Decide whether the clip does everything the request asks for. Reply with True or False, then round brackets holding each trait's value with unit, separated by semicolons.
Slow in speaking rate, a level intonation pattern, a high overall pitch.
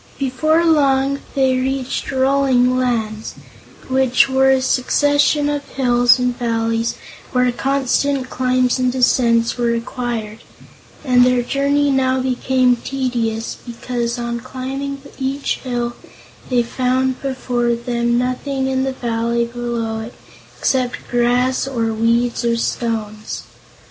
True (120 wpm; 1.9 semitones; 250 Hz)